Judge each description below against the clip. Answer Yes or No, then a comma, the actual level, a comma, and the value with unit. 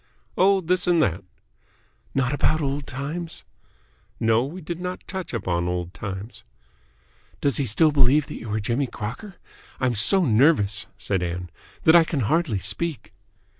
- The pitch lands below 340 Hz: Yes, low, 135 Hz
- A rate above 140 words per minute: Yes, average, 155 wpm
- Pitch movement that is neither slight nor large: No, wide, 7.8 semitones